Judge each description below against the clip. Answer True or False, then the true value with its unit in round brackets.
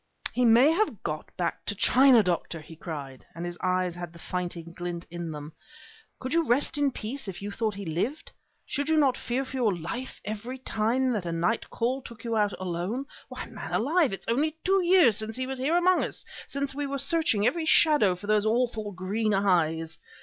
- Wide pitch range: True (7.0 semitones)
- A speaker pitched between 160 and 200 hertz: False (220 Hz)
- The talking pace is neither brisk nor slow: False (215 wpm)